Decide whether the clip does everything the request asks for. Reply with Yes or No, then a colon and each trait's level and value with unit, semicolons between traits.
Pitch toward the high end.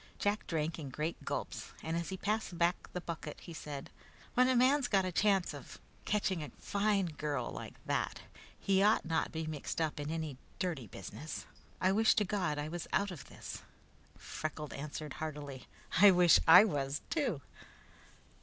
No: medium, 170 Hz